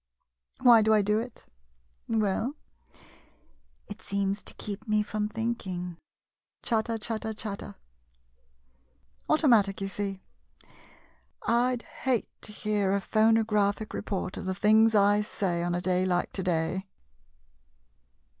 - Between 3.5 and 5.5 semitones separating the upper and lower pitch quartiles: No, average, 2.7 semitones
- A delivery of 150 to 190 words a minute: No, average, 140 wpm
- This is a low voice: No, high, 205 Hz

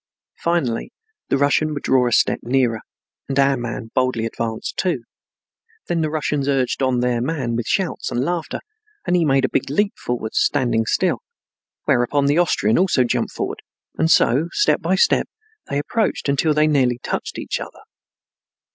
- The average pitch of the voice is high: No, low, 135 Hz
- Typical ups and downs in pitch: Yes, average, 4.3 semitones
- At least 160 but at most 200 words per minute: Yes, average, 170 wpm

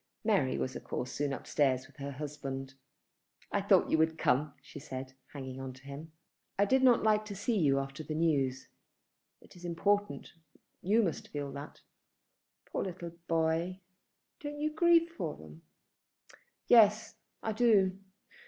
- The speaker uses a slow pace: No, average, 155 wpm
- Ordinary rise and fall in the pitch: No, wide, 7.0 semitones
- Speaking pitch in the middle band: Yes, medium, 160 Hz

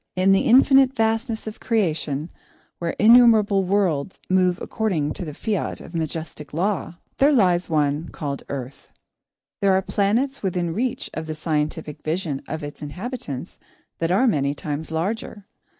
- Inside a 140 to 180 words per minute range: Yes, average, 150 wpm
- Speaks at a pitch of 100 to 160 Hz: No, medium, 180 Hz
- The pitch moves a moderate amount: No, wide, 5.9 semitones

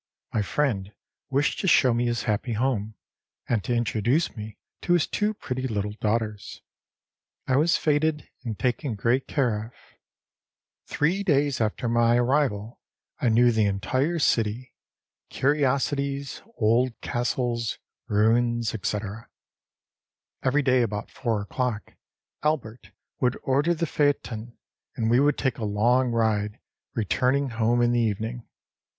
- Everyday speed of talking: No, slow, 130 wpm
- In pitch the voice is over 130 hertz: No, low, 120 Hz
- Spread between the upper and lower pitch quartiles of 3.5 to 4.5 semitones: Yes, average, 3.8 semitones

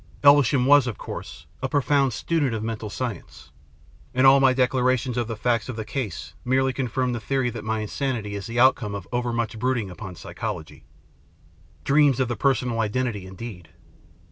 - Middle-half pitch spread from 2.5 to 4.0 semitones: Yes, average, 3.3 semitones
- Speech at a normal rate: Yes, average, 175 wpm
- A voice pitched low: Yes, low, 120 Hz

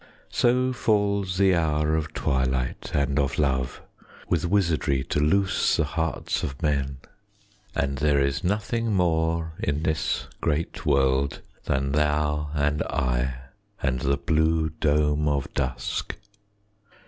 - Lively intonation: No, average, 3.1 semitones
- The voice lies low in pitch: Yes, very low, 75 Hz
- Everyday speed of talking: No, slow, 125 wpm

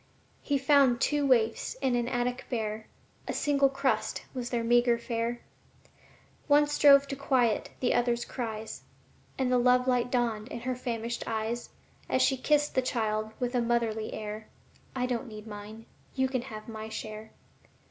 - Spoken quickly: No, average, 165 wpm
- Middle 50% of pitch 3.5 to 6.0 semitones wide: No, average, 2.7 semitones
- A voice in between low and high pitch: No, high, 240 Hz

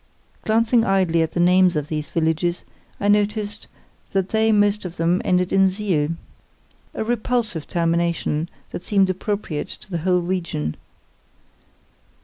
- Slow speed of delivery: Yes, slow, 130 wpm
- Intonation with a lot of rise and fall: No, average, 3.7 semitones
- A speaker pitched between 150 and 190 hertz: Yes, medium, 185 Hz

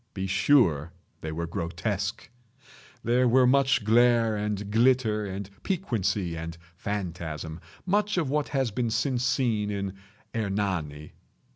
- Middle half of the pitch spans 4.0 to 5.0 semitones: No, wide, 5.4 semitones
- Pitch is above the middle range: No, low, 105 Hz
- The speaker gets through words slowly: Yes, slow, 120 wpm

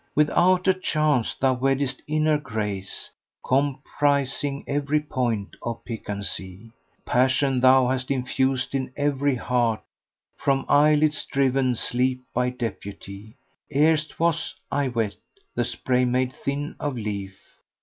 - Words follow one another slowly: Yes, slow, 125 wpm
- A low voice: Yes, low, 130 Hz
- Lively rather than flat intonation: No, average, 2.9 semitones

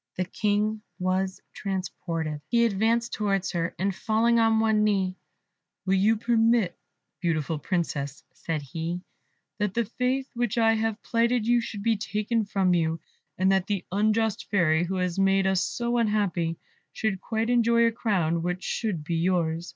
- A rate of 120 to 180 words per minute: Yes, average, 160 wpm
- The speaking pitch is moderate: No, high, 200 Hz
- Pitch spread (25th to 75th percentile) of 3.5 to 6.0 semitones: Yes, average, 4.0 semitones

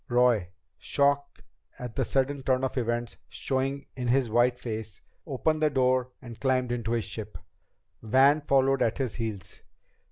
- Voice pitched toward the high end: No, low, 125 Hz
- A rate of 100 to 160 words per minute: Yes, average, 155 wpm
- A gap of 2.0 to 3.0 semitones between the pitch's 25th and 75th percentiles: Yes, narrow, 2.5 semitones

